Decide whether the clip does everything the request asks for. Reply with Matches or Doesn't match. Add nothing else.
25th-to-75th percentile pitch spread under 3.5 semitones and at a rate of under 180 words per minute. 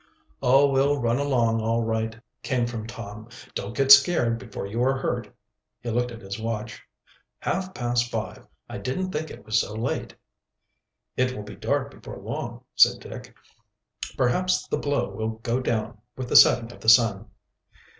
Matches